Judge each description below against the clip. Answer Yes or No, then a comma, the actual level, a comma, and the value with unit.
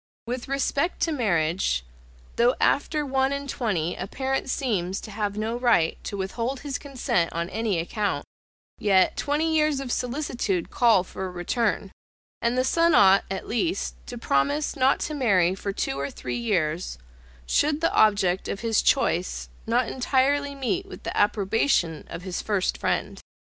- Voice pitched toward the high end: Yes, high, 225 Hz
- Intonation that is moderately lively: No, wide, 6.2 semitones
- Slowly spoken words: No, average, 165 wpm